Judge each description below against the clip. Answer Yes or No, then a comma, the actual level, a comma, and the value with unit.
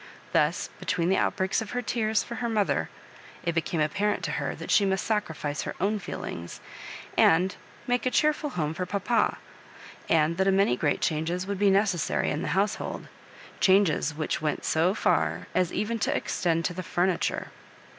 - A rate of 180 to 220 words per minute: Yes, average, 185 wpm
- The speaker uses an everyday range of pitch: Yes, average, 4.2 semitones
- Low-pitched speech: No, medium, 185 Hz